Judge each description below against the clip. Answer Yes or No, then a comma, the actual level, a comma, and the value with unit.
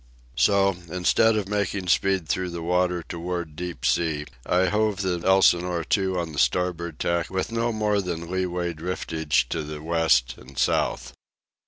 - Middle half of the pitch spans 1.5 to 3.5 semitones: Yes, narrow, 2.6 semitones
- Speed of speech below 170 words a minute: Yes, average, 160 wpm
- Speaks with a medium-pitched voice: No, very low, 90 Hz